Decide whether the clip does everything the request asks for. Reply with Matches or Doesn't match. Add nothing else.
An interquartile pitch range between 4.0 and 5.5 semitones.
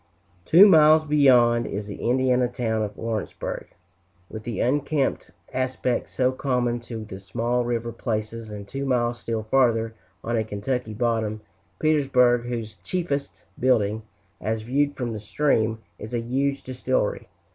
Doesn't match